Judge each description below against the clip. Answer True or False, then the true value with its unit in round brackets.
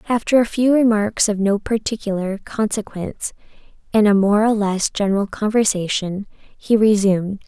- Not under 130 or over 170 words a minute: True (135 wpm)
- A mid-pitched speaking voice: False (210 Hz)